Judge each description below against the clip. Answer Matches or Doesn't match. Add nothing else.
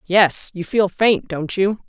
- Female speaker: Matches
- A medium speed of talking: Matches